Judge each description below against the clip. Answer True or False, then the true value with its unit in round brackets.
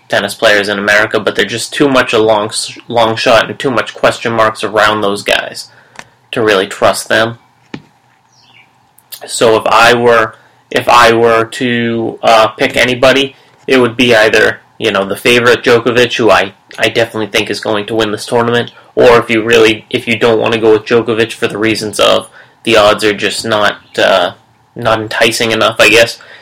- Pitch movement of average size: False (1.4 semitones)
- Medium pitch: False (115 Hz)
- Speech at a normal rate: True (190 wpm)